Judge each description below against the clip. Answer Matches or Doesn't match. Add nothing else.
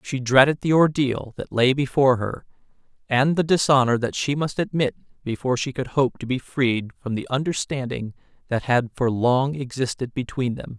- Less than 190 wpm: Matches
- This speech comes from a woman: Doesn't match